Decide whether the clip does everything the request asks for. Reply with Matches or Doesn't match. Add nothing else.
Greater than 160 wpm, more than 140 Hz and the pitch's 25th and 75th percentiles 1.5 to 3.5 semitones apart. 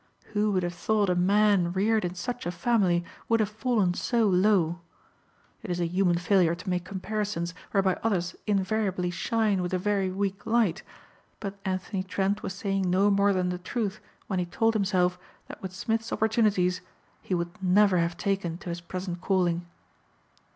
Matches